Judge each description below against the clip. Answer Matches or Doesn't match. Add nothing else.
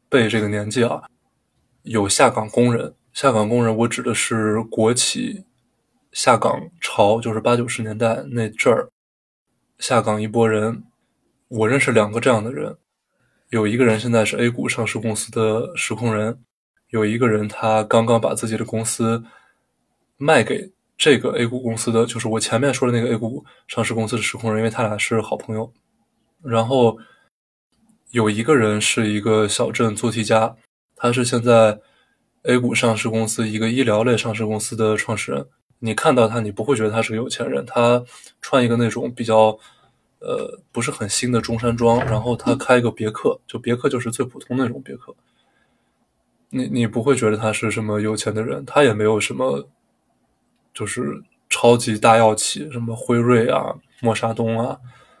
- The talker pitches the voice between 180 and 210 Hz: Doesn't match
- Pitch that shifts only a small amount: Matches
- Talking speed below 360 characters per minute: Matches